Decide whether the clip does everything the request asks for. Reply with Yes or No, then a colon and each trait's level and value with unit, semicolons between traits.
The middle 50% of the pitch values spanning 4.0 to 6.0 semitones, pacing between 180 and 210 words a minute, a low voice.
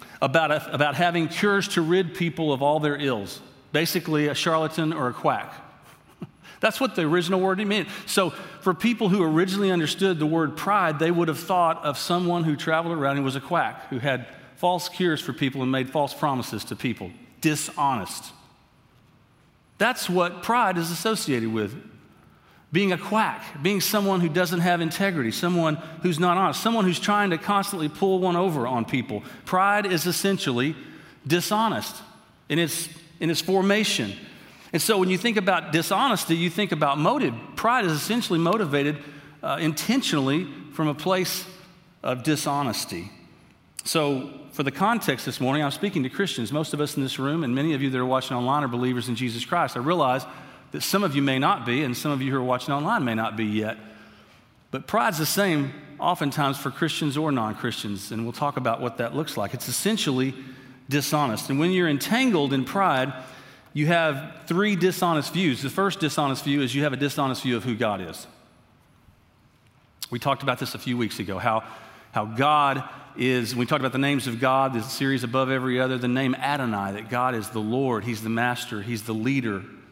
No: wide, 5.4 semitones; average, 190 wpm; medium, 150 Hz